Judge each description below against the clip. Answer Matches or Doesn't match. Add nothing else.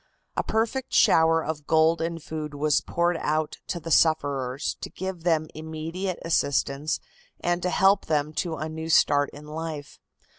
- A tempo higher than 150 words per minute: Matches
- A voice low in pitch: Doesn't match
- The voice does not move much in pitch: Matches